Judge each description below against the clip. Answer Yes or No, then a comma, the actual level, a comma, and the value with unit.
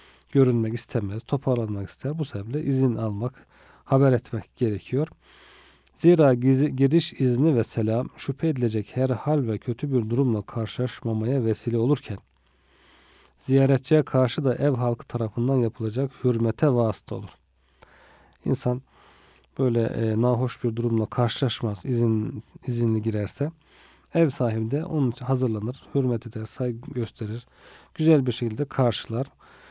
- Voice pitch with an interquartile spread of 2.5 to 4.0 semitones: Yes, average, 3.3 semitones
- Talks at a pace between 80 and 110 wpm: No, average, 125 wpm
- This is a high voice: No, low, 125 Hz